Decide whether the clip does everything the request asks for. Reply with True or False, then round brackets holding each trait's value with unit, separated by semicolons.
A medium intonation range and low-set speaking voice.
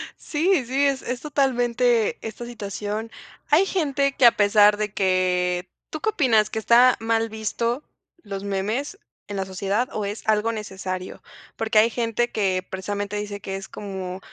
False (3.5 semitones; 220 Hz)